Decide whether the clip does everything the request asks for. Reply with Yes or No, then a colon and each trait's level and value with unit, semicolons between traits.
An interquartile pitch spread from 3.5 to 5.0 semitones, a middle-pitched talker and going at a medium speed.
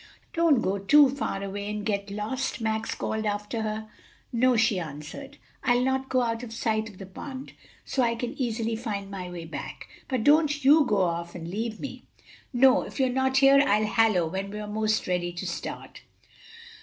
No: average, 4.6 semitones; high, 220 Hz; average, 190 wpm